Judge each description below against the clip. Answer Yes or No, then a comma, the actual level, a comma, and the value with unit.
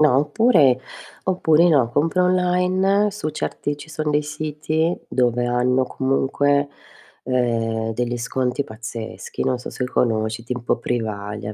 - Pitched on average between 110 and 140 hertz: Yes, low, 135 Hz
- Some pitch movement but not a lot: Yes, average, 4.5 semitones